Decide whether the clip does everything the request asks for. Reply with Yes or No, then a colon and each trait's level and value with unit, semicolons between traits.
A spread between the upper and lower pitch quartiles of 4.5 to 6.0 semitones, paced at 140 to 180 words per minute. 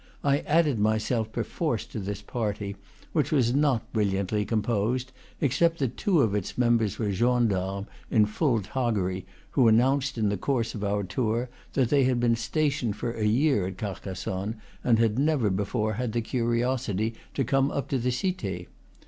No: average, 3.8 semitones; average, 170 wpm